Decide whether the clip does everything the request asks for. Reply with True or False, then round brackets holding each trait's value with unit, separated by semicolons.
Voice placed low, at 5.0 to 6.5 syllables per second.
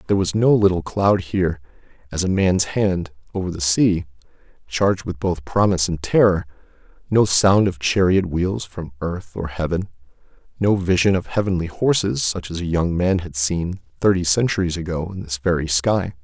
True (90 Hz; 5.1 syllables/s)